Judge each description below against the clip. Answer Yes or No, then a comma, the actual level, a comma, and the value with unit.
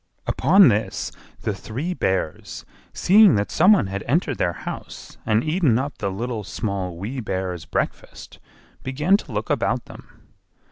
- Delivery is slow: No, average, 150 wpm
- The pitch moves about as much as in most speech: No, wide, 8.2 semitones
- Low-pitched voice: Yes, low, 115 Hz